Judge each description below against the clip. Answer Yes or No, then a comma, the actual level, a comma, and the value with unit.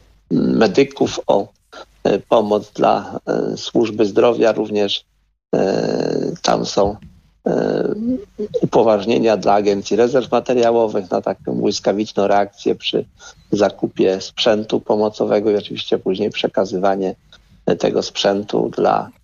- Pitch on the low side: Yes, low, 105 Hz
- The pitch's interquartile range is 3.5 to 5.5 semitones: No, average, 2.8 semitones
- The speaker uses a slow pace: Yes, slow, 90 wpm